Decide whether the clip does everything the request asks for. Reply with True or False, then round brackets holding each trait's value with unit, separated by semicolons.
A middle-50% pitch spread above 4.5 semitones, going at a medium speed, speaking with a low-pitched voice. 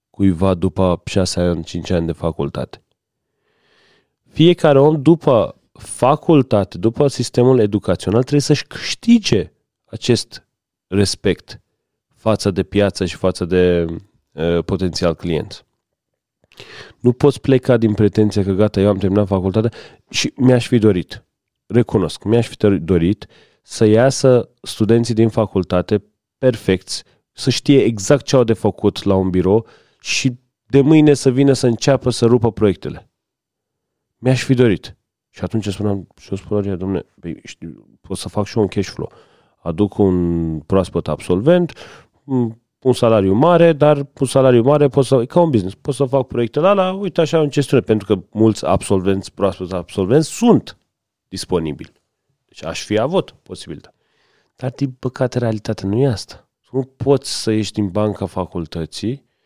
True (5.3 semitones; 145 wpm; 110 Hz)